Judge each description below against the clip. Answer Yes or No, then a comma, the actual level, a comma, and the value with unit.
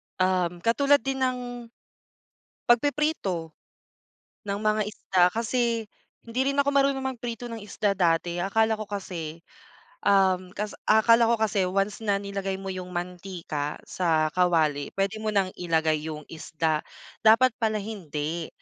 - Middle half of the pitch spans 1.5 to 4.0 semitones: No, average, 4.7 semitones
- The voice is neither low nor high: No, high, 200 Hz